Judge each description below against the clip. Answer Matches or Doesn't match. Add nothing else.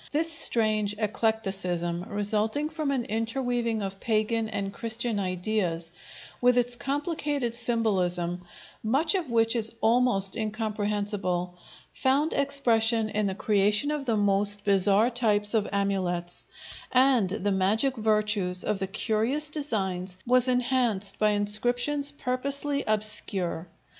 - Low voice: Doesn't match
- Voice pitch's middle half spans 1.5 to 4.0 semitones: Matches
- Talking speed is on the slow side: Matches